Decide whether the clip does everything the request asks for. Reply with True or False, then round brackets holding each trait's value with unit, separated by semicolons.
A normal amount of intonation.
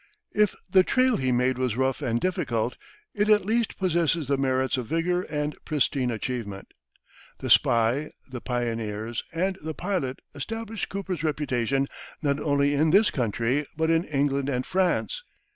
False (6.0 semitones)